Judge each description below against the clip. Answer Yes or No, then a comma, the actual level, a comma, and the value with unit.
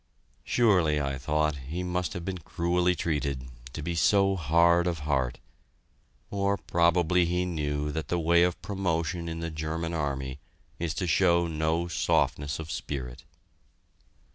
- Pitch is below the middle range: Yes, very low, 85 Hz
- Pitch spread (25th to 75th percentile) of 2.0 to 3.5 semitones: Yes, average, 2.8 semitones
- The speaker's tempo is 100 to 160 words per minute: Yes, average, 145 wpm